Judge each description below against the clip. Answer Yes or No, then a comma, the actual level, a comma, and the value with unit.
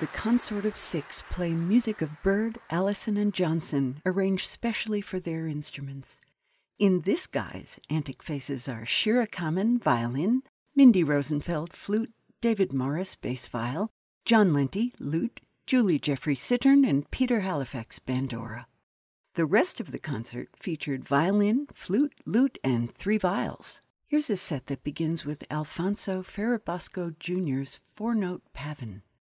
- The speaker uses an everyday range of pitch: No, wide, 7.5 semitones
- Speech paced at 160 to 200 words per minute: No, slow, 135 wpm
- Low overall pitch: No, medium, 175 Hz